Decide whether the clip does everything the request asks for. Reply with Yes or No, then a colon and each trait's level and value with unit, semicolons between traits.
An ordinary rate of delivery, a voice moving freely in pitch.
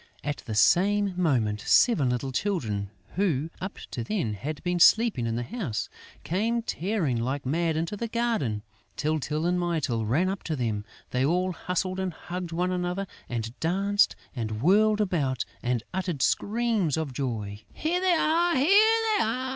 Yes: average, 165 wpm; wide, 8.0 semitones